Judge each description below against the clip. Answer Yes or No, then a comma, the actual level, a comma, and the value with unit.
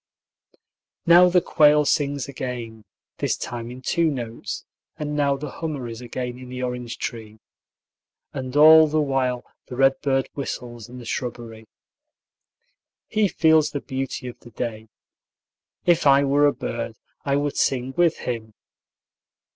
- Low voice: Yes, low, 130 Hz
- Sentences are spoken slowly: No, average, 145 wpm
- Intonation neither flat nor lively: Yes, average, 3.4 semitones